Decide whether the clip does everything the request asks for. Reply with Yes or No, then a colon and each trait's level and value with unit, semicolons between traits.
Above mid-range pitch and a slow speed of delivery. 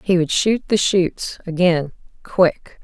No: medium, 175 Hz; slow, 125 wpm